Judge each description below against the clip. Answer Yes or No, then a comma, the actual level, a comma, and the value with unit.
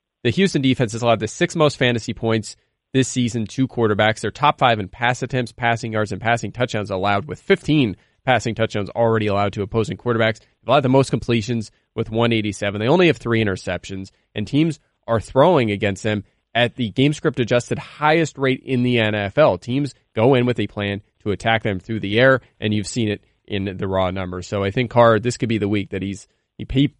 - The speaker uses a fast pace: Yes, fast, 215 wpm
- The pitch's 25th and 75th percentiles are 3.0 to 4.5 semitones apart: Yes, average, 3.5 semitones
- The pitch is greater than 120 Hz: No, low, 115 Hz